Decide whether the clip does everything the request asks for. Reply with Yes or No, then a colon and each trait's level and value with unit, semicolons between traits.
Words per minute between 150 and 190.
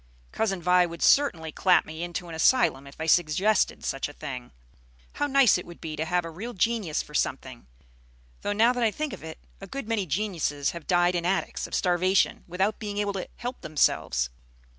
No: fast, 205 wpm